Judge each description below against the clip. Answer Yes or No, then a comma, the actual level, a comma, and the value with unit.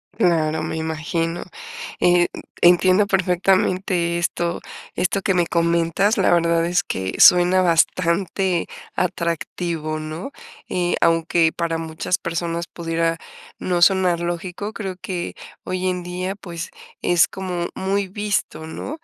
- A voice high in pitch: No, medium, 175 Hz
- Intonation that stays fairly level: Yes, narrow, 1.8 semitones